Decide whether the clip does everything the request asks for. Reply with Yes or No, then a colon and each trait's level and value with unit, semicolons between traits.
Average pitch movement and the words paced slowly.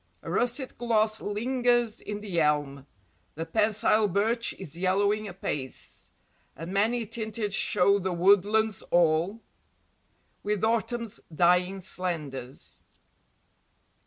Yes: average, 4.0 semitones; slow, 100 wpm